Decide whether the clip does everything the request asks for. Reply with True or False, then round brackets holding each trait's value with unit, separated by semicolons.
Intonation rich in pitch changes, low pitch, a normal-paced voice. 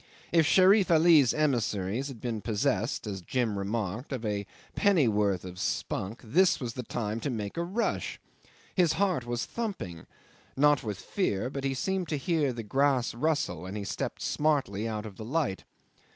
True (6.7 semitones; 125 Hz; 170 wpm)